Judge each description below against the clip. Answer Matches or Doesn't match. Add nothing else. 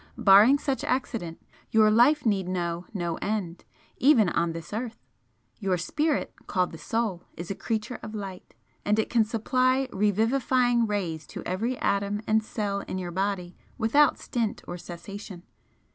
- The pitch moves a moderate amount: Matches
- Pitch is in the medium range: Doesn't match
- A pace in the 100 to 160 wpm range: Matches